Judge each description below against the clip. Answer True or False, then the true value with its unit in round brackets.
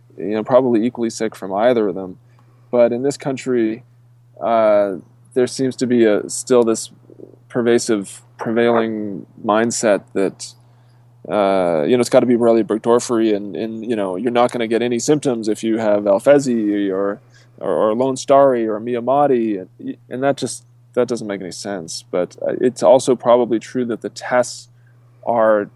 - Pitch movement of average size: False (2.1 semitones)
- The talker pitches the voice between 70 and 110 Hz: False (120 Hz)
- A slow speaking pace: False (170 wpm)